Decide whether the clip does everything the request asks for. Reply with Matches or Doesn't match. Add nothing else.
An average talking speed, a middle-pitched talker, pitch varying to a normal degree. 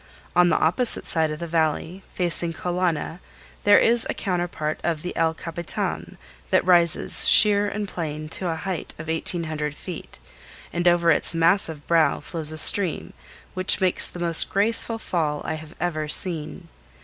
Doesn't match